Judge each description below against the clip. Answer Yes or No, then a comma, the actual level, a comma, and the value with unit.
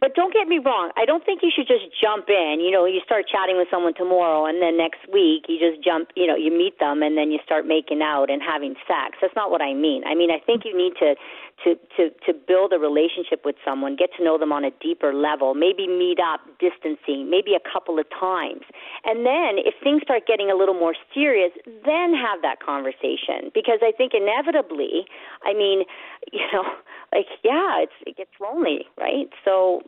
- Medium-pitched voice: Yes, medium, 180 Hz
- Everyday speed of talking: No, fast, 220 wpm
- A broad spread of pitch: Yes, wide, 6.8 semitones